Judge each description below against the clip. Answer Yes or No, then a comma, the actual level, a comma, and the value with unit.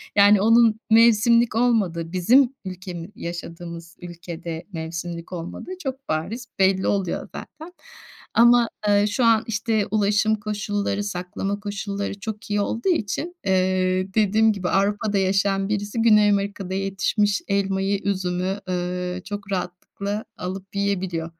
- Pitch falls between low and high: No, high, 200 Hz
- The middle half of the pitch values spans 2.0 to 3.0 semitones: Yes, narrow, 2.6 semitones